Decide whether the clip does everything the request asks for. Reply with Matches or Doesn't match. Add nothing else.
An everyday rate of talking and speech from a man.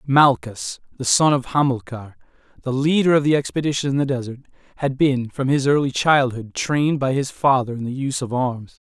Matches